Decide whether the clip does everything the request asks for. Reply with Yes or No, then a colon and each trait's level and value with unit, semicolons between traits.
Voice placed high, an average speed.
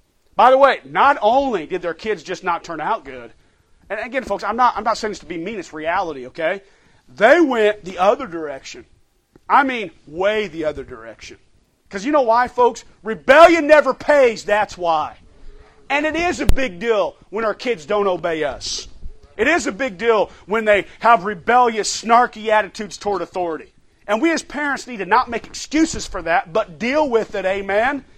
Yes: high, 215 Hz; average, 190 wpm